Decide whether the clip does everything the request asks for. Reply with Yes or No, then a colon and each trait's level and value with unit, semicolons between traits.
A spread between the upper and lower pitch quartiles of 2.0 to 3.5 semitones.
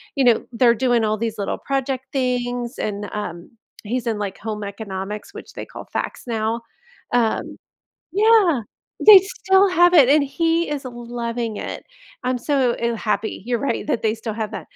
No: average, 4.0 semitones